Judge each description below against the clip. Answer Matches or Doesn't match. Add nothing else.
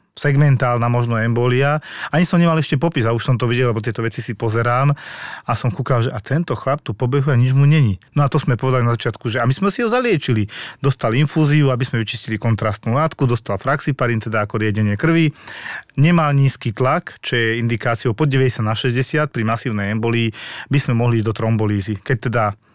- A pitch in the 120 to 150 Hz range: Matches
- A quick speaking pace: Matches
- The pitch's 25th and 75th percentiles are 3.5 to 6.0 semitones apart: Matches